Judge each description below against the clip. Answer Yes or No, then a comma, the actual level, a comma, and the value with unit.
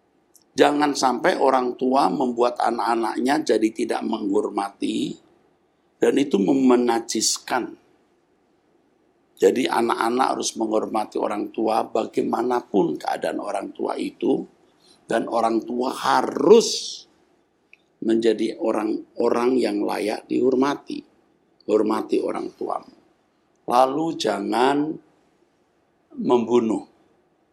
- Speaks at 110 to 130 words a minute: No, slow, 85 wpm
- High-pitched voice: Yes, very high, 320 Hz